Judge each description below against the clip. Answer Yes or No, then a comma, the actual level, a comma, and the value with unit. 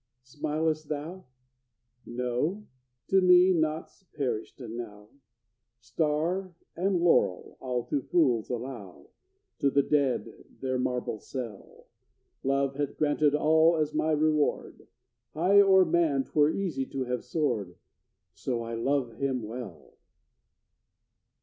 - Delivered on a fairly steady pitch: No, average, 4.3 semitones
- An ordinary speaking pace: No, slow, 115 wpm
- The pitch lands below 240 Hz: Yes, medium, 140 Hz